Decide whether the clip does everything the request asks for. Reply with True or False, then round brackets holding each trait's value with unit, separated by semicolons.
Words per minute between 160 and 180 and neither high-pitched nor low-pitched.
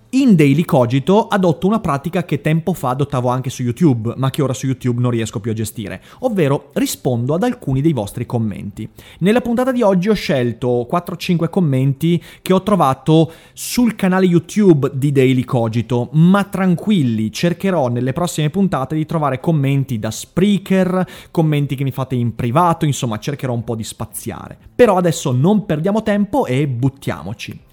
True (165 wpm; 150 Hz)